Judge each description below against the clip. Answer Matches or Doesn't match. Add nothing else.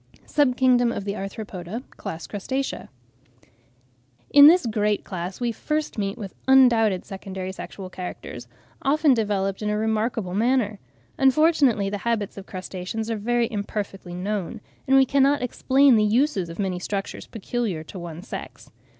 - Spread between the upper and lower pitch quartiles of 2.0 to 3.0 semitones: Doesn't match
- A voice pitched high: Matches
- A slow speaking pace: Doesn't match